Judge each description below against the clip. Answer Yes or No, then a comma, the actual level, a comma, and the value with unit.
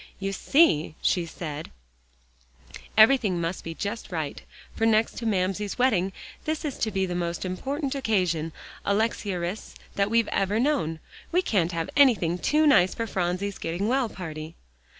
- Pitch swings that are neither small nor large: Yes, average, 4.8 semitones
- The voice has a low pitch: No, high, 195 Hz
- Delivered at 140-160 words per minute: Yes, average, 155 wpm